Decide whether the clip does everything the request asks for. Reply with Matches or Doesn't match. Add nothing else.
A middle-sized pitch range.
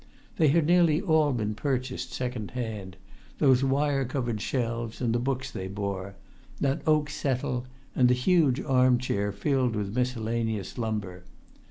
Matches